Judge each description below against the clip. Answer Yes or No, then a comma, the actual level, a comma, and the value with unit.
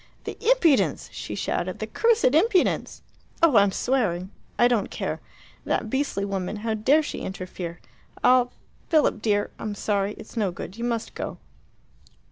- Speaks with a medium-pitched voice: No, high, 225 Hz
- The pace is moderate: Yes, average, 150 wpm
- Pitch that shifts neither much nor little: No, wide, 5.9 semitones